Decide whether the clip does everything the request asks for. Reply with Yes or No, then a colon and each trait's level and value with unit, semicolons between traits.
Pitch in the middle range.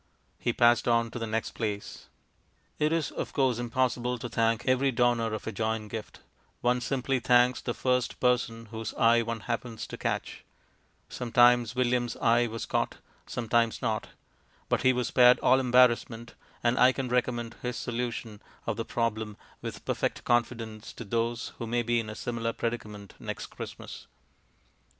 No: low, 120 Hz